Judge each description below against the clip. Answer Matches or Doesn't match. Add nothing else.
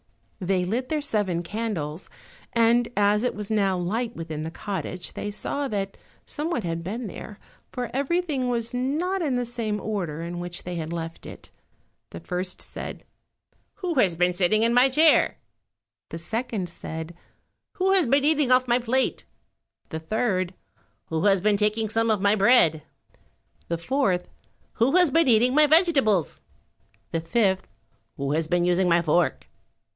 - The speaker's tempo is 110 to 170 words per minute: Matches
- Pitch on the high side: Matches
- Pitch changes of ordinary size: Doesn't match